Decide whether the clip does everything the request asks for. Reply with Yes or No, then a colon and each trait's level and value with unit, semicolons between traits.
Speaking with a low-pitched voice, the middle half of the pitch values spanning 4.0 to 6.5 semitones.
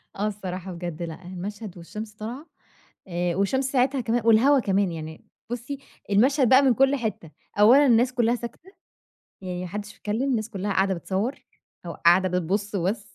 No: high, 210 Hz; average, 4.7 semitones